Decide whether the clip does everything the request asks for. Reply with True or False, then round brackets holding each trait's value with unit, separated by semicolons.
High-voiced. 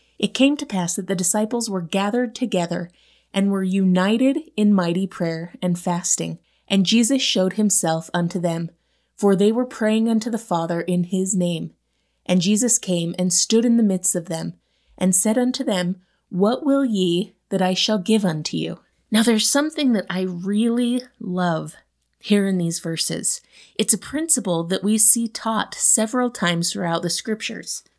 True (195 Hz)